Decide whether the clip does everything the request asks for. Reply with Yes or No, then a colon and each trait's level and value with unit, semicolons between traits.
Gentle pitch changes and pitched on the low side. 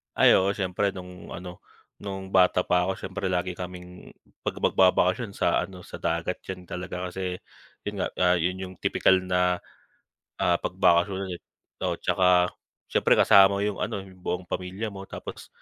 Yes: narrow, 1.1 semitones; very low, 90 Hz